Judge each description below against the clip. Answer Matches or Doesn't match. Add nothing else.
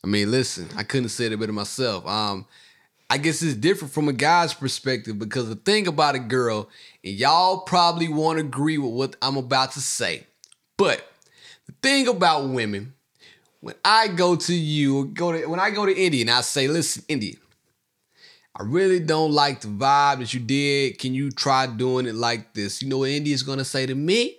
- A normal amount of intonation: Matches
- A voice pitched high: Doesn't match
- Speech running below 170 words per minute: Doesn't match